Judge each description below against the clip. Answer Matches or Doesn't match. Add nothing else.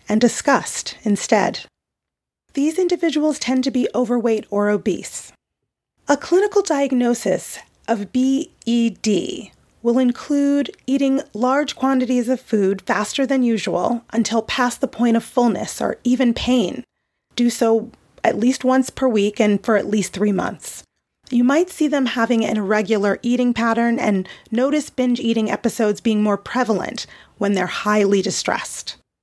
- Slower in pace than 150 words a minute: Matches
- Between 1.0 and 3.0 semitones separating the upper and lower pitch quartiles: Doesn't match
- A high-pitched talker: Matches